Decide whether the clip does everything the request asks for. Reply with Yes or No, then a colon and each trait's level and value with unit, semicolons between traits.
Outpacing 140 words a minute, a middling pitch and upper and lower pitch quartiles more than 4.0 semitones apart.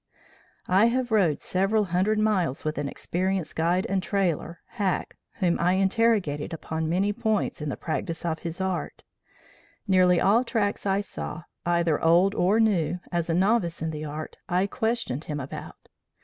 No: average, 165 wpm; medium, 180 Hz; average, 3.7 semitones